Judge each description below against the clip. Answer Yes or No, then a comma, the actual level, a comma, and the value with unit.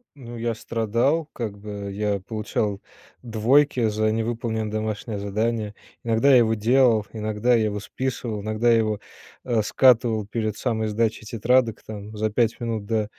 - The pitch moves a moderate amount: No, narrow, 1.8 semitones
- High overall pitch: No, low, 110 Hz